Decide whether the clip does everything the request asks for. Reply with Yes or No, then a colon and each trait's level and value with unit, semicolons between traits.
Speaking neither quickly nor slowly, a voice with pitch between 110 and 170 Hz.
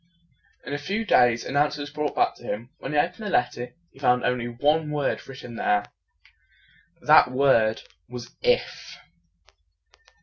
Yes: average, 160 wpm; low, 135 Hz